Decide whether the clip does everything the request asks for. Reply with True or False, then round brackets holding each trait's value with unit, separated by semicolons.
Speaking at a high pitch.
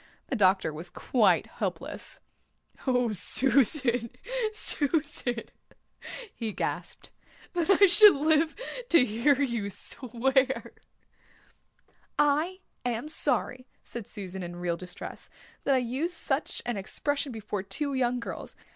True (250 Hz)